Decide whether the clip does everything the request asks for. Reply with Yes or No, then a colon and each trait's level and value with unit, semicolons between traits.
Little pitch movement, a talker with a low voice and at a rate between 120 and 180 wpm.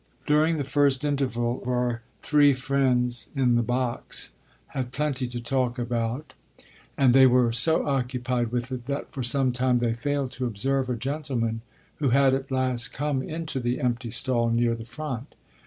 Yes: narrow, 2.2 semitones; low, 125 Hz; average, 170 wpm